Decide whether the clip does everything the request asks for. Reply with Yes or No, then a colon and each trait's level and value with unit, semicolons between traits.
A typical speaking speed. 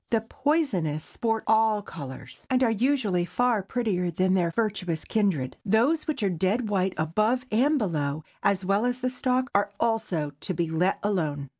Yes: average, 170 wpm